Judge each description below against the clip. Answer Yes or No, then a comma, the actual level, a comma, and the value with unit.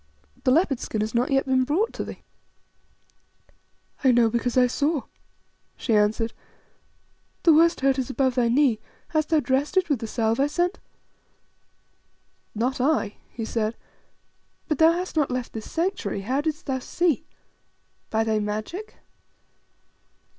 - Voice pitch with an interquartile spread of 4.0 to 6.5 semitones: Yes, average, 5.2 semitones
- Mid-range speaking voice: No, very high, 260 Hz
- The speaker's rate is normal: Yes, average, 150 wpm